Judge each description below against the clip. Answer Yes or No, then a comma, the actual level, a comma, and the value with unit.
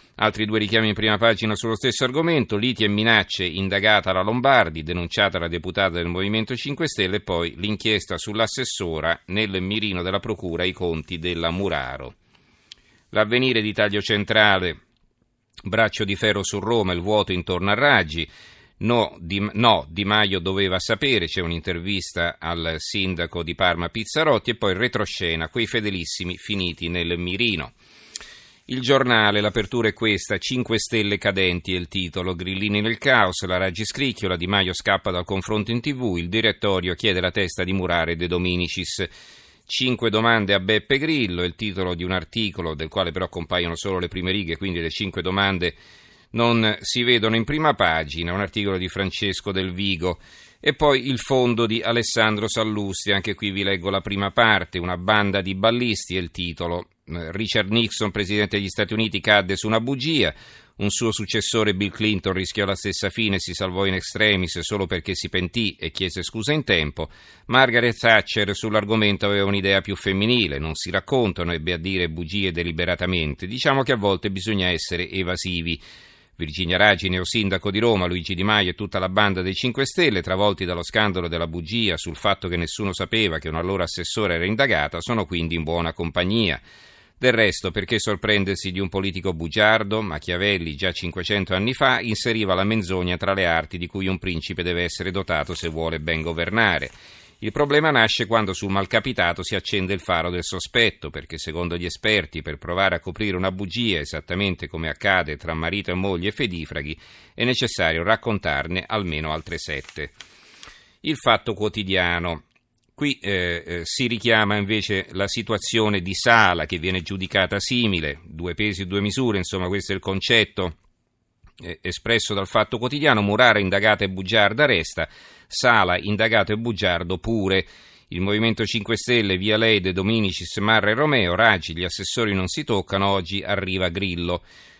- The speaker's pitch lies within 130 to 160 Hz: No, low, 100 Hz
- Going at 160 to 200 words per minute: Yes, fast, 170 wpm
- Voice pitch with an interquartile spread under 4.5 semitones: Yes, average, 3.5 semitones